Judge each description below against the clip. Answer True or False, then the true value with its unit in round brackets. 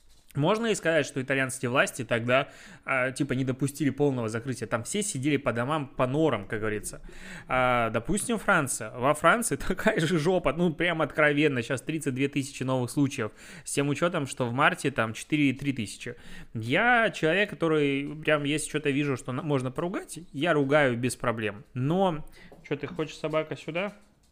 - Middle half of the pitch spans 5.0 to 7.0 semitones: False (3.8 semitones)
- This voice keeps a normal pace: False (165 wpm)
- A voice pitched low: False (145 Hz)